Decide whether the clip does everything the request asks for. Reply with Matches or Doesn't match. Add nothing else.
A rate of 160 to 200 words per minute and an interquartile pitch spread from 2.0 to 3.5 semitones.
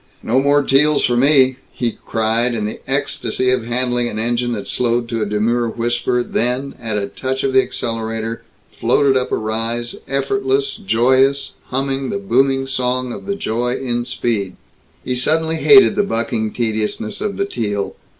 Matches